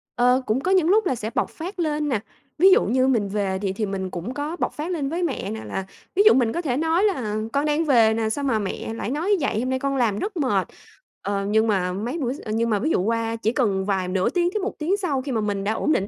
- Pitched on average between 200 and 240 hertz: No, very high, 250 Hz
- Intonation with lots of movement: Yes, wide, 6.6 semitones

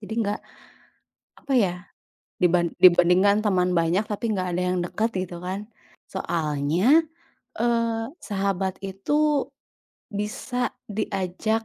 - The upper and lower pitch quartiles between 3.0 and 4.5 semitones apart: Yes, average, 3.5 semitones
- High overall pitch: Yes, high, 195 Hz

